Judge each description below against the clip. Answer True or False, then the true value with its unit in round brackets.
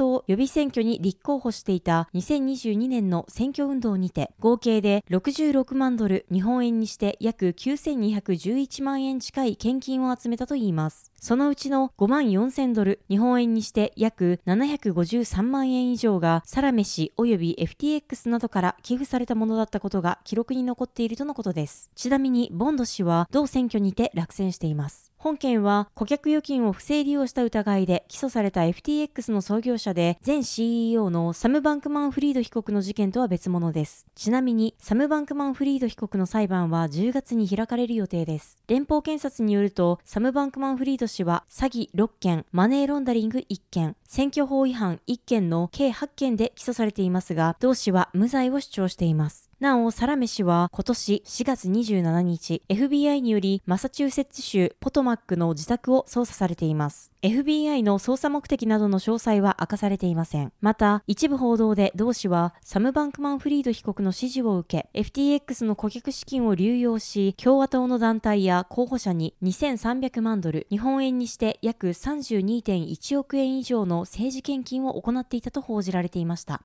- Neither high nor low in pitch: False (230 Hz)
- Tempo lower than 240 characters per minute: False (330 characters per minute)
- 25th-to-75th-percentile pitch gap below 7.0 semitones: True (5.5 semitones)